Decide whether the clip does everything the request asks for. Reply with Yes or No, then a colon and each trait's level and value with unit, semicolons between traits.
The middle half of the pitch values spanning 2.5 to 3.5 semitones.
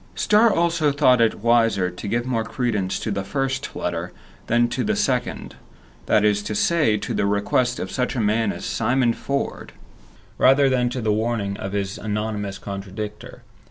No: average, 4.0 semitones